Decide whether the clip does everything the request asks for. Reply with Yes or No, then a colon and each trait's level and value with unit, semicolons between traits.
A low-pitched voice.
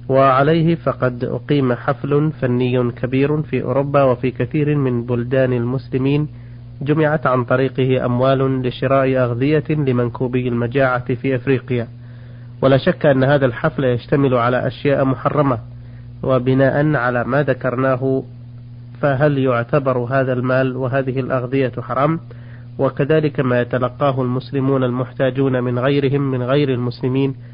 Yes: low, 130 Hz